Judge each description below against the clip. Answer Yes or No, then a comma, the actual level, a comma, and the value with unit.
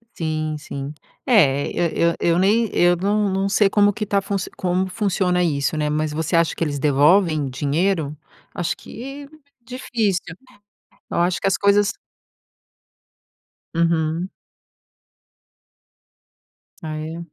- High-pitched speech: No, medium, 175 Hz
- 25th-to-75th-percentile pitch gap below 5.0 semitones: Yes, average, 4.3 semitones